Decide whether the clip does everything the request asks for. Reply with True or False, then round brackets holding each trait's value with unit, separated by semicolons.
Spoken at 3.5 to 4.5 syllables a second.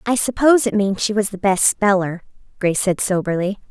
False (5.7 syllables/s)